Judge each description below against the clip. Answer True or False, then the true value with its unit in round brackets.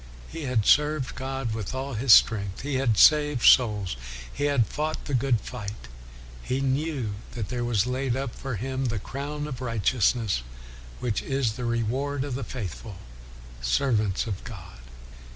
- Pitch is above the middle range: False (125 Hz)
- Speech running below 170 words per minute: True (160 wpm)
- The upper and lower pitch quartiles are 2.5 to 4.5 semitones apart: True (3.8 semitones)